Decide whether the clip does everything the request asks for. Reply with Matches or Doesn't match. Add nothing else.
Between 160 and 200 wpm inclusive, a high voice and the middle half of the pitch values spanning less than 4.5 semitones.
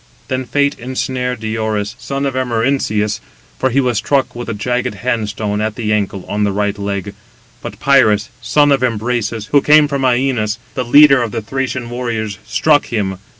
Doesn't match